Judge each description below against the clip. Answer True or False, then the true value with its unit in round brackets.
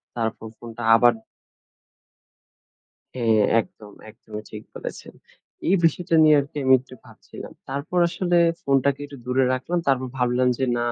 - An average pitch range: True (3.2 semitones)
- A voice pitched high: False (130 Hz)